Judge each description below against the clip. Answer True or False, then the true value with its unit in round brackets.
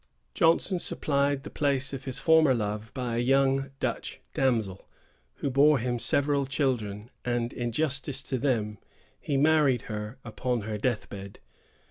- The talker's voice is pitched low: True (130 Hz)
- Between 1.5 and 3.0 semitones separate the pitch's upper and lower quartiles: False (3.6 semitones)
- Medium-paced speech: True (150 wpm)